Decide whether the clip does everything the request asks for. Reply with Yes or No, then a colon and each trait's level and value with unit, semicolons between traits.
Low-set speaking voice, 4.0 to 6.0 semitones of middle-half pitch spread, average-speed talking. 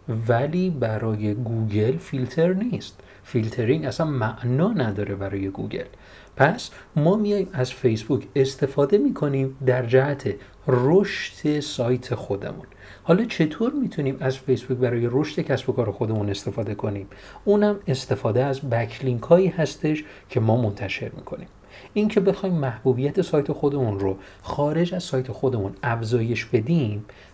Yes: low, 130 Hz; average, 5.1 semitones; average, 125 wpm